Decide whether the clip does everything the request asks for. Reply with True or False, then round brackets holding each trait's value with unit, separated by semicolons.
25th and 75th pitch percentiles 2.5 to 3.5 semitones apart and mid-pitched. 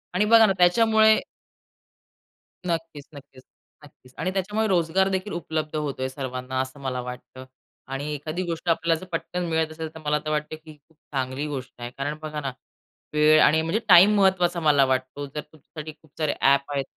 False (3.9 semitones; 155 Hz)